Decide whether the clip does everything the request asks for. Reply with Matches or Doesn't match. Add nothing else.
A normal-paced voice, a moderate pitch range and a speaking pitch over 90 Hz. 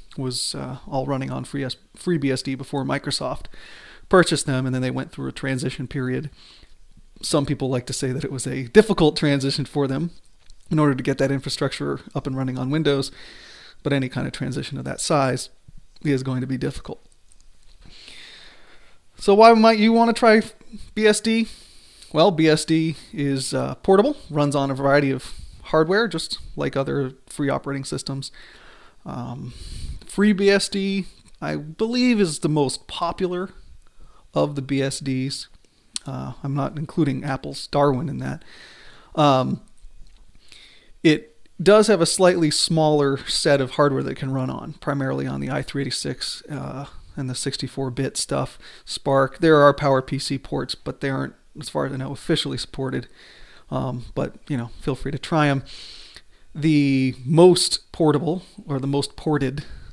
Matches